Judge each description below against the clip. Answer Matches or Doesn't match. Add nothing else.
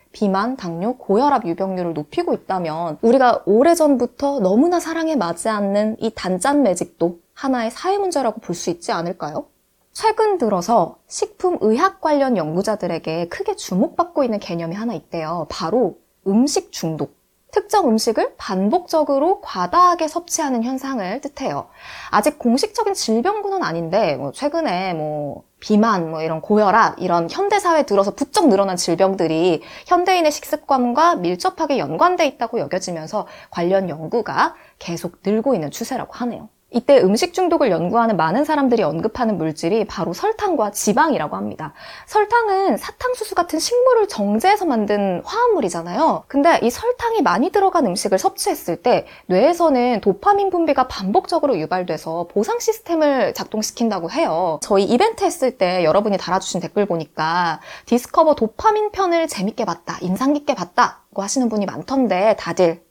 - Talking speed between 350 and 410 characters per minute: Matches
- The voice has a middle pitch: Doesn't match